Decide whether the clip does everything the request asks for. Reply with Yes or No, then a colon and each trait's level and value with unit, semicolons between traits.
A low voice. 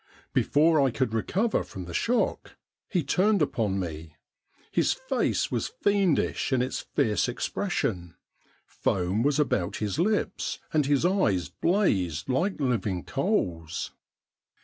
Yes: low, 130 Hz